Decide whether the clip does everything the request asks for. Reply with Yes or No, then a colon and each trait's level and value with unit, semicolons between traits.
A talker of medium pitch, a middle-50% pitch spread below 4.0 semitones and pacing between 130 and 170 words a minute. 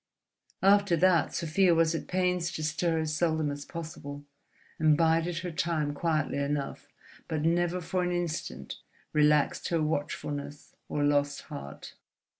Yes: medium, 160 Hz; average, 2.8 semitones; average, 140 wpm